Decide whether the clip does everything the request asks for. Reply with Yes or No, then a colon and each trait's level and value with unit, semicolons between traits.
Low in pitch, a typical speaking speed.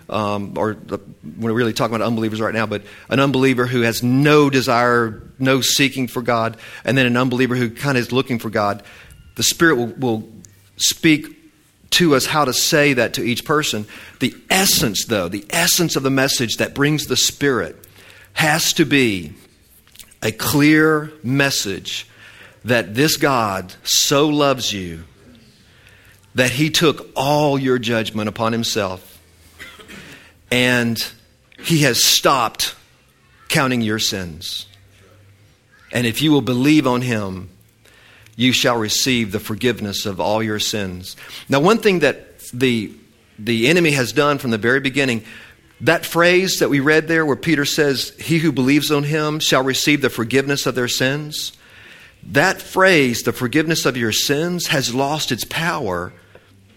Yes: low, 125 Hz; average, 155 wpm